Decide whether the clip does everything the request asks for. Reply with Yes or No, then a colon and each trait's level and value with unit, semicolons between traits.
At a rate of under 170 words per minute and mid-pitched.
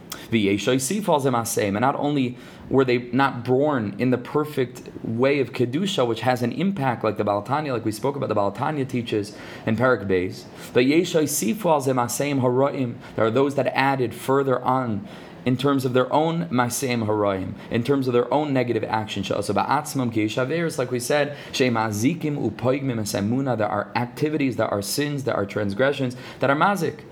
No: average, 140 wpm; low, 125 Hz